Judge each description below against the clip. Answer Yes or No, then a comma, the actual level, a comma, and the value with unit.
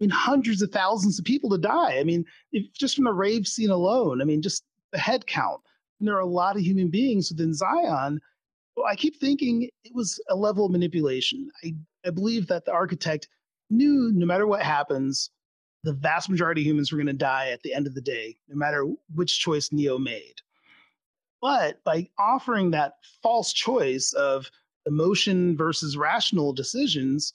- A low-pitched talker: No, medium, 180 Hz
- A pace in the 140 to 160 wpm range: No, average, 190 wpm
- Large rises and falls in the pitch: Yes, wide, 6.8 semitones